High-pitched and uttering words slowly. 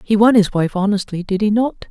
No: high, 205 Hz; fast, 220 wpm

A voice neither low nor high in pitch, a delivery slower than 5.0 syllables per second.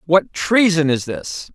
Yes: medium, 155 Hz; 3.6 syllables/s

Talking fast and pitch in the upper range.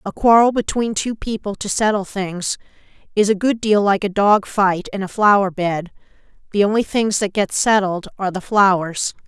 No: average, 190 wpm; high, 200 Hz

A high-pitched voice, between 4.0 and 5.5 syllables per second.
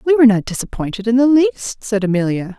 No: high, 225 Hz; 6.0 syllables/s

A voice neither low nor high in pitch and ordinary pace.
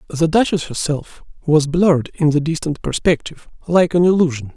Yes: medium, 160 Hz; average, 160 wpm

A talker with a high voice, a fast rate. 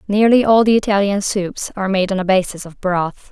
Yes: high, 195 Hz; fast, 215 wpm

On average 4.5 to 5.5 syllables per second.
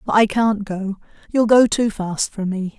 No: 4.2 syllables/s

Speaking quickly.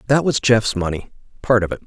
No: average, 195 wpm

